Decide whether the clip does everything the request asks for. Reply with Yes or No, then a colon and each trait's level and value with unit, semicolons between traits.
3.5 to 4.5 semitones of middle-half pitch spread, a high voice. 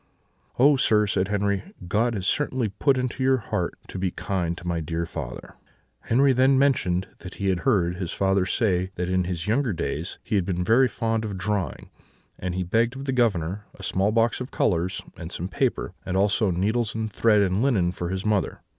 No: average, 4.2 semitones; low, 100 Hz